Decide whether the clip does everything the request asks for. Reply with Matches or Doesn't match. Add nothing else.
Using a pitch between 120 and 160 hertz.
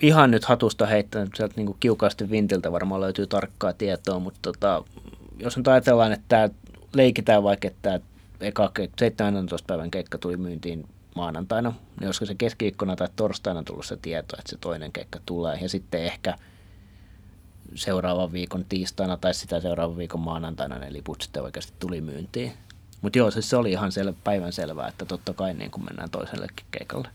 Doesn't match